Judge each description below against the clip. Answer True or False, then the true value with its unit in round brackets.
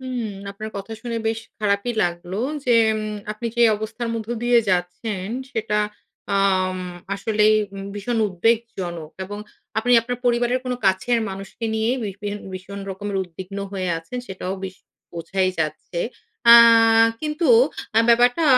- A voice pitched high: True (210 Hz)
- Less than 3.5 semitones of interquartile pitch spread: False (3.8 semitones)